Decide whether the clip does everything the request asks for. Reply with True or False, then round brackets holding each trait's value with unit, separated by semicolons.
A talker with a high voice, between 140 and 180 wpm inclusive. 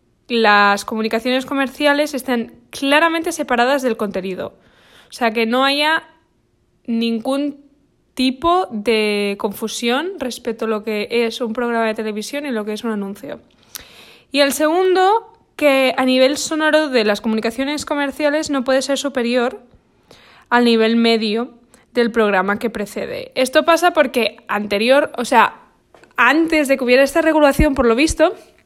True (255 Hz; 145 wpm)